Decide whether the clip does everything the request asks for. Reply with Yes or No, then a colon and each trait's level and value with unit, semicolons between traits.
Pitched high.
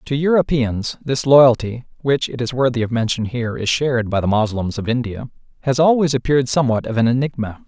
No: low, 125 Hz